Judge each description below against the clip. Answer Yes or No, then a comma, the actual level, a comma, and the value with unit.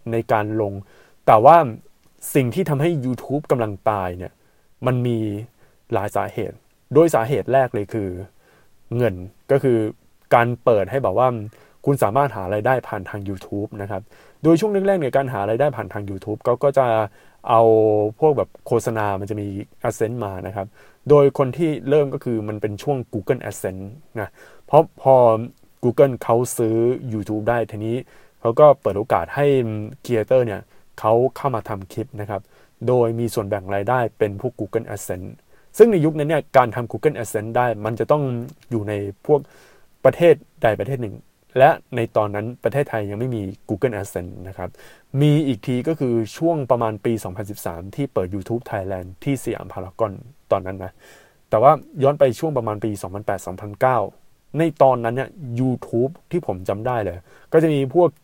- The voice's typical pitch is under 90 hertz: No, low, 115 Hz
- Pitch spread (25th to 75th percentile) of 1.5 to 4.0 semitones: No, average, 4.4 semitones